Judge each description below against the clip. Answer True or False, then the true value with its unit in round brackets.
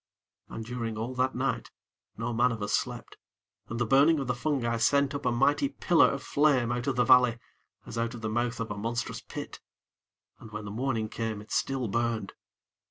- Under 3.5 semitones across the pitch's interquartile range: True (2.8 semitones)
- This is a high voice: False (120 Hz)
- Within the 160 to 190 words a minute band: False (205 wpm)